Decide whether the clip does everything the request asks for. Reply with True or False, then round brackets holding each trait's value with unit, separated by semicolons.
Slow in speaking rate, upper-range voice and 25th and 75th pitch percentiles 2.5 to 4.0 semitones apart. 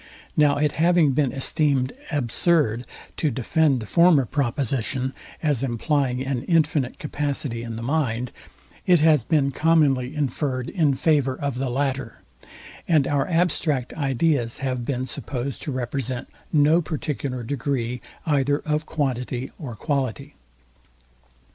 False (130 wpm; 140 Hz; 3.1 semitones)